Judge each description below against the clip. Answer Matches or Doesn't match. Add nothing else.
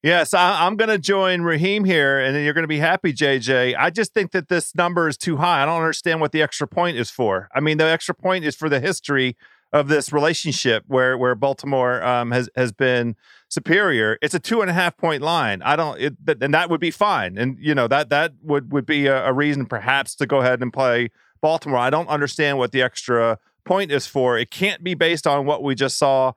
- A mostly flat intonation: Doesn't match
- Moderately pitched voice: Matches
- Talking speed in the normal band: Doesn't match